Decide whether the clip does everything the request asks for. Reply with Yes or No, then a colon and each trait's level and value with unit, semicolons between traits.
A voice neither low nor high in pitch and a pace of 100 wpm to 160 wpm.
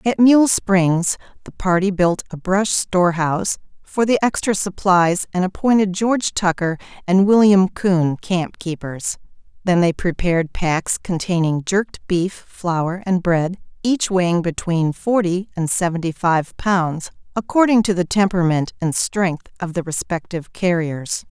Yes: medium, 180 Hz; average, 145 wpm